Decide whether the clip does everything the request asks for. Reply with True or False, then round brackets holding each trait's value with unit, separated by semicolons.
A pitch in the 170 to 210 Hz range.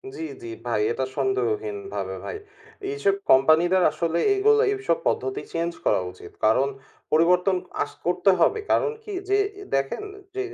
True (190 Hz)